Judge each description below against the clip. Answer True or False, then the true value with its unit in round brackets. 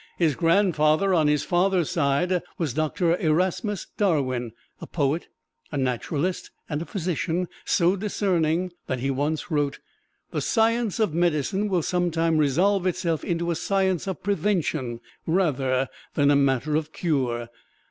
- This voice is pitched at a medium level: True (165 Hz)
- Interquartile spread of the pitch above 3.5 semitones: True (4.1 semitones)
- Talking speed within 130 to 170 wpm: True (145 wpm)